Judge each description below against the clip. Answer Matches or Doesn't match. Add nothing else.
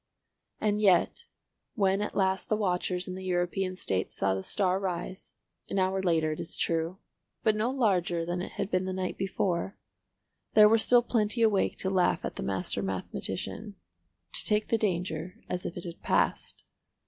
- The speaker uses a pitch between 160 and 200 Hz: Matches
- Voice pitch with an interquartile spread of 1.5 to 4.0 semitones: Matches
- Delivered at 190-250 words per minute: Doesn't match